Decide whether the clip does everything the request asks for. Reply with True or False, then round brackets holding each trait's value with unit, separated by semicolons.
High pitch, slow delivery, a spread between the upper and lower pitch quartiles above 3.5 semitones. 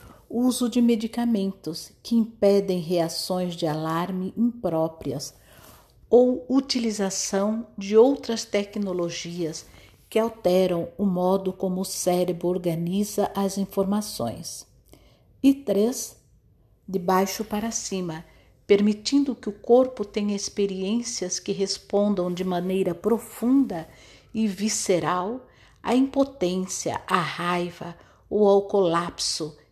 True (195 Hz; 100 wpm; 4.0 semitones)